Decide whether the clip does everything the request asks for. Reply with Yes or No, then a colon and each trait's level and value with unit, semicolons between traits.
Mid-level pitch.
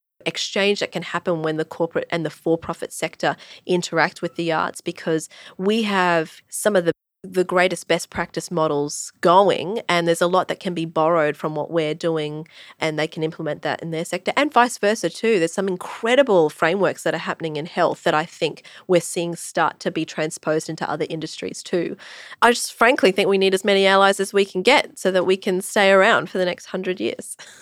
Yes: medium, 175 Hz